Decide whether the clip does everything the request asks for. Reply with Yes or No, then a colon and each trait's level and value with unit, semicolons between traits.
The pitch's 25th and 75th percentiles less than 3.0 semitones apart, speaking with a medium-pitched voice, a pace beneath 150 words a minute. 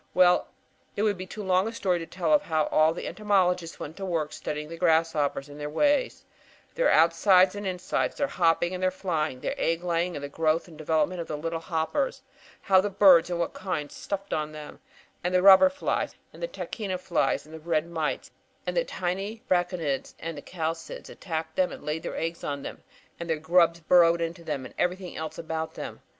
No: narrow, 2.6 semitones; medium, 170 Hz; fast, 205 wpm